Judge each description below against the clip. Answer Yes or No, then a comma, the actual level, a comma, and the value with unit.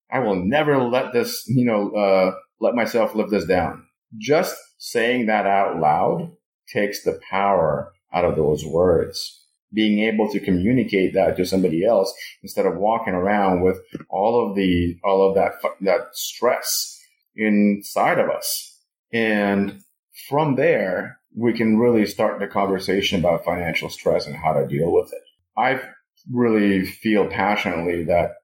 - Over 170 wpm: No, average, 150 wpm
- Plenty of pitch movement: Yes, wide, 5.9 semitones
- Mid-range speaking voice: No, low, 105 Hz